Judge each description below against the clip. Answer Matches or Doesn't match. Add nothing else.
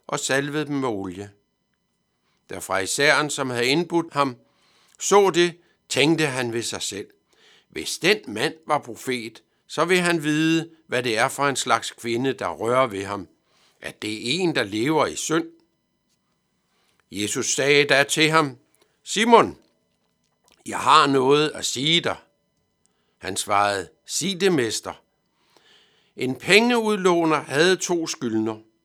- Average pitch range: Doesn't match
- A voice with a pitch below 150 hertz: Matches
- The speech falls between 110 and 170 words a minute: Matches